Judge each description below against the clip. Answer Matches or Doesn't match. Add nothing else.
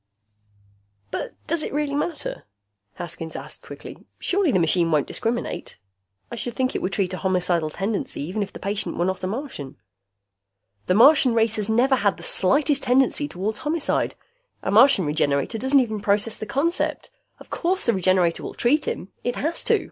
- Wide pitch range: Matches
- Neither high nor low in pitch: Doesn't match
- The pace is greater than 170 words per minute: Matches